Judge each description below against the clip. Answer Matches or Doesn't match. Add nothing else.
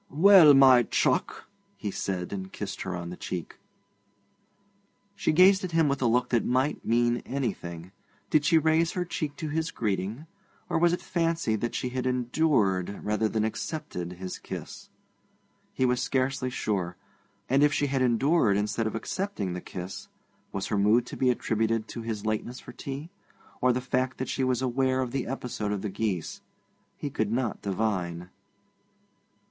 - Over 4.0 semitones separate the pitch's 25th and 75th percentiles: Matches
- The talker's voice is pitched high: Doesn't match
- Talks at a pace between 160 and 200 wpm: Matches